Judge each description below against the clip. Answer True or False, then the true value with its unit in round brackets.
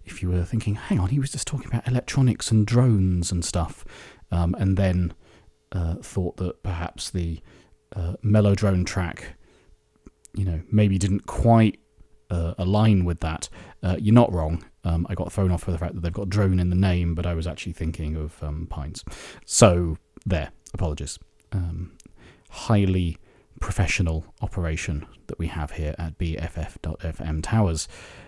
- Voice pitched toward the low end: True (90 Hz)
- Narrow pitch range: False (3.3 semitones)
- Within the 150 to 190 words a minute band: True (165 wpm)